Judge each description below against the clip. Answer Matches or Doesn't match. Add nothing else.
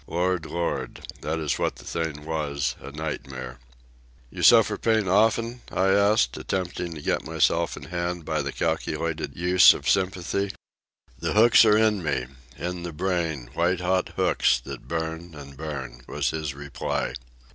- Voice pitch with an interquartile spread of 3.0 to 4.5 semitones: Matches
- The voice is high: Doesn't match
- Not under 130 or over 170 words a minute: Matches